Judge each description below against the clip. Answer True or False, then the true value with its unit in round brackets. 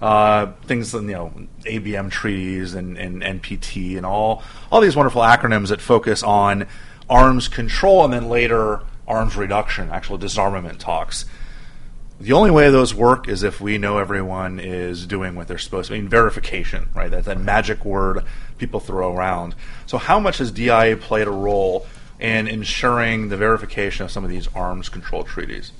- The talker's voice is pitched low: True (105 Hz)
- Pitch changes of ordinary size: True (3.2 semitones)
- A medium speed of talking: True (170 wpm)